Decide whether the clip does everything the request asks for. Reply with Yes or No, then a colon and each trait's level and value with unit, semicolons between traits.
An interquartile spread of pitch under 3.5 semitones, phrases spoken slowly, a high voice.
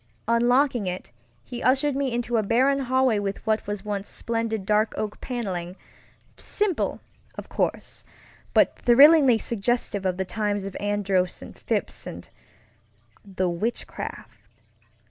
No: average, 3.8 semitones; slow, 125 wpm; high, 220 Hz